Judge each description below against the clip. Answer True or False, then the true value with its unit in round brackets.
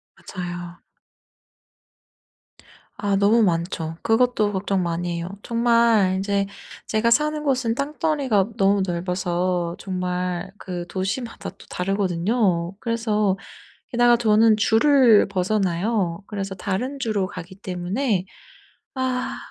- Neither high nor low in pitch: False (200 Hz)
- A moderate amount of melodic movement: True (4.3 semitones)